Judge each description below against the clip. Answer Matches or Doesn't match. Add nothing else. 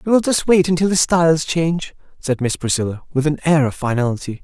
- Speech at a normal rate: Doesn't match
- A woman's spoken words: Doesn't match